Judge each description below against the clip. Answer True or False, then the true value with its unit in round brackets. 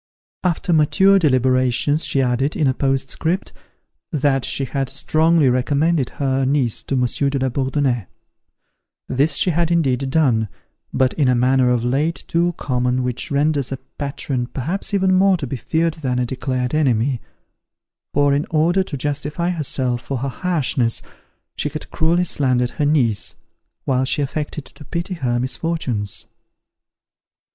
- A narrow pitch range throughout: False (3.8 semitones)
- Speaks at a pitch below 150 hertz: True (140 Hz)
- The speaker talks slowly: False (150 wpm)